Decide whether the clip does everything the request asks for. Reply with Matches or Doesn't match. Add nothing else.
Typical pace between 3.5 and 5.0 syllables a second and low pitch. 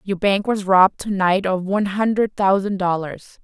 Doesn't match